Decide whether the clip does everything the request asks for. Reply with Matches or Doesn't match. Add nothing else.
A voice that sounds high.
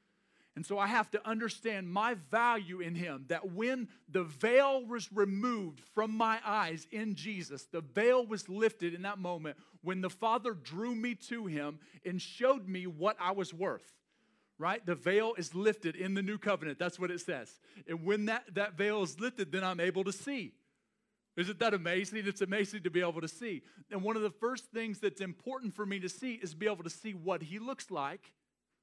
Matches